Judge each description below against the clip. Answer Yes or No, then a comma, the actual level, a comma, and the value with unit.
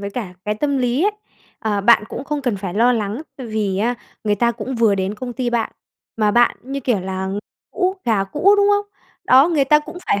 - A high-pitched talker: Yes, high, 235 Hz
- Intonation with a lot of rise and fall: No, average, 4.8 semitones